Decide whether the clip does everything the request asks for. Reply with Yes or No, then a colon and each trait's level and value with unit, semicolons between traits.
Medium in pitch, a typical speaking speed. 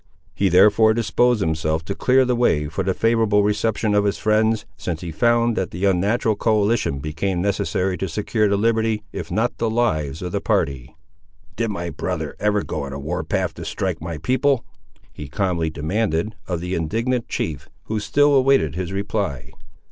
No: low, 100 Hz; average, 180 wpm